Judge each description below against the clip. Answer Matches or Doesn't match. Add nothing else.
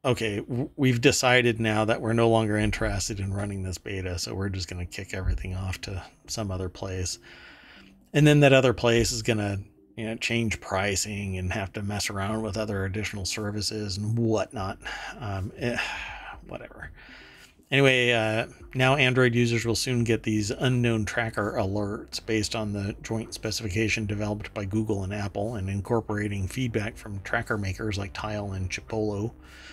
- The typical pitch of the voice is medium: Doesn't match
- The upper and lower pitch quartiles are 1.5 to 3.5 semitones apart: Matches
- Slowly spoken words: Doesn't match